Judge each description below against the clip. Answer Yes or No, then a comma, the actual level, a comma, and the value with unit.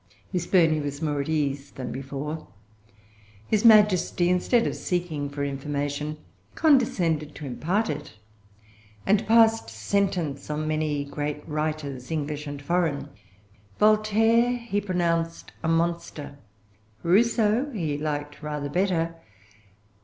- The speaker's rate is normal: No, slow, 115 wpm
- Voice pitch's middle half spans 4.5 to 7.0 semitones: Yes, average, 5.0 semitones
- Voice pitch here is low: No, medium, 155 Hz